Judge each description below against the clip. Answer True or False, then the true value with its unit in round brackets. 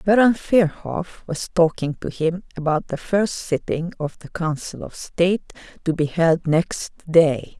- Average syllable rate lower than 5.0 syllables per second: True (4.1 syllables/s)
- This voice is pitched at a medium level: True (170 Hz)